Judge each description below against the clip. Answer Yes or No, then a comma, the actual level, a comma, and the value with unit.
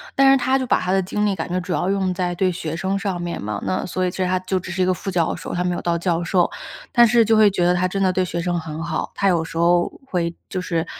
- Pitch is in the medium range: Yes, medium, 180 Hz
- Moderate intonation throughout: No, narrow, 2.0 semitones